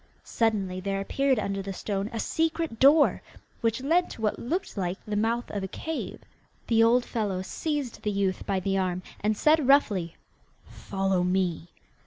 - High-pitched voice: Yes, high, 210 Hz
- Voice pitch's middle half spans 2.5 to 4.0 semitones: No, average, 5.0 semitones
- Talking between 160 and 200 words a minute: Yes, average, 170 wpm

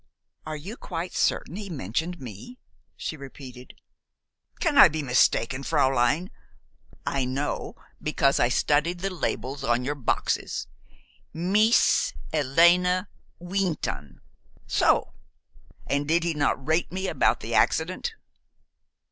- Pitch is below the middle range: No, medium, 155 Hz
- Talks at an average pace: No, slow, 115 wpm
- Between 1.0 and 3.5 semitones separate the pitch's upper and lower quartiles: No, average, 5.1 semitones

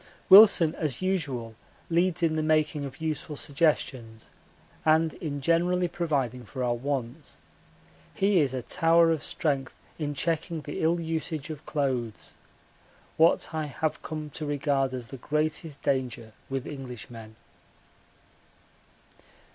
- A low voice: No, medium, 150 Hz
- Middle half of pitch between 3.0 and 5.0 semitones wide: Yes, average, 3.6 semitones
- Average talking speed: No, slow, 130 wpm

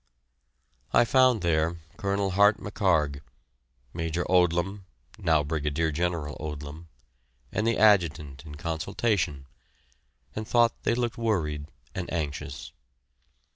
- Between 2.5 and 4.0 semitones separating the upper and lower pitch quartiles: No, average, 5.1 semitones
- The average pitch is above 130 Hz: No, very low, 85 Hz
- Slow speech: Yes, slow, 105 wpm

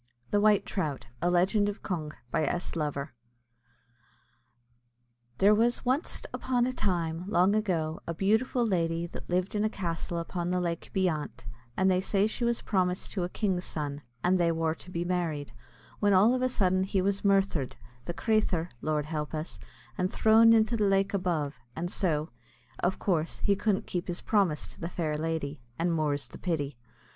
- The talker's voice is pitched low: No, medium, 180 Hz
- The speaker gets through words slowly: No, average, 180 wpm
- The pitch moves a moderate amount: Yes, average, 3.7 semitones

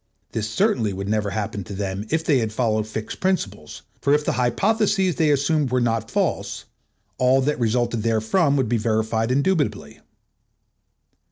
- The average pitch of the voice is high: No, low, 120 Hz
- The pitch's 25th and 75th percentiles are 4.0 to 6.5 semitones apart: Yes, average, 4.8 semitones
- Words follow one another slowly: No, average, 165 wpm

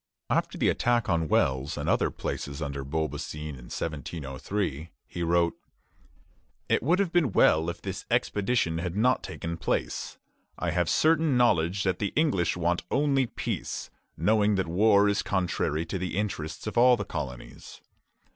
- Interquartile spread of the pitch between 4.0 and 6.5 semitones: Yes, average, 5.2 semitones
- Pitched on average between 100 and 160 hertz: No, very low, 90 Hz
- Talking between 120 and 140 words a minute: No, average, 155 wpm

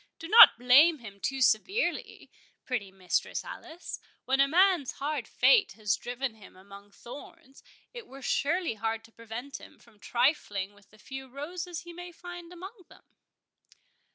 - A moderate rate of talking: Yes, average, 155 wpm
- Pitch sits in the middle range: No, very high, 270 Hz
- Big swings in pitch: Yes, wide, 7.5 semitones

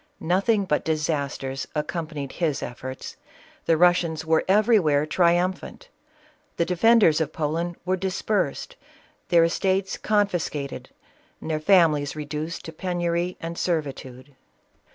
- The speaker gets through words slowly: Yes, slow, 110 wpm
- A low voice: No, medium, 165 Hz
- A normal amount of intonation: Yes, average, 3.3 semitones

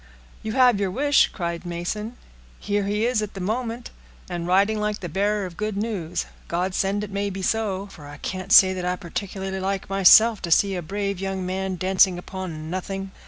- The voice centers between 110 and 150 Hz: No, high, 195 Hz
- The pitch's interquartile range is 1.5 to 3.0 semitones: Yes, narrow, 2.4 semitones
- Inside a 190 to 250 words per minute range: Yes, average, 200 wpm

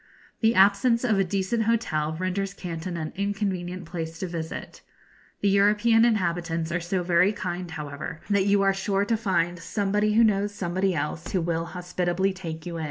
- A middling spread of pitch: Yes, average, 3.1 semitones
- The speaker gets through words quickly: No, average, 175 wpm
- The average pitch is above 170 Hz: Yes, medium, 185 Hz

